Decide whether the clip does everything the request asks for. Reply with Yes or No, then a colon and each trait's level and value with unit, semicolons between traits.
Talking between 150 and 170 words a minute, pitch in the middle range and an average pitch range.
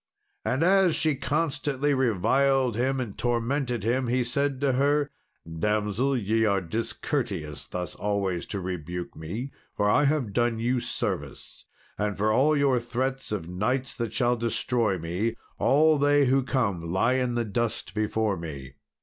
No: average, 155 wpm; low, 120 Hz; average, 4.8 semitones